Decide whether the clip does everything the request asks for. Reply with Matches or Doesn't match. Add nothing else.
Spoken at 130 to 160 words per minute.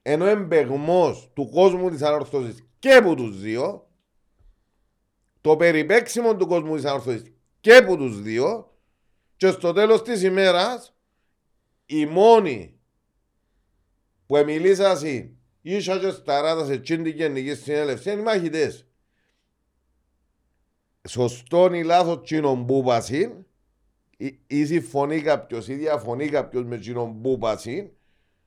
Doesn't match